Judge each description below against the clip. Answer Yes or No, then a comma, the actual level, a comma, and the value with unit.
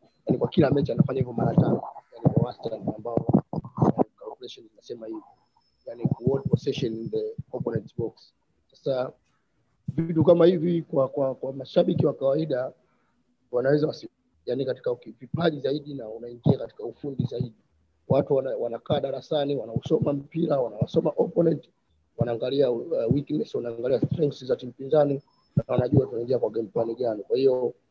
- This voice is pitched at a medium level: Yes, medium, 150 Hz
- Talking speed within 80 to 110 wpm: Yes, slow, 100 wpm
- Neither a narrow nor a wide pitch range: Yes, average, 4.8 semitones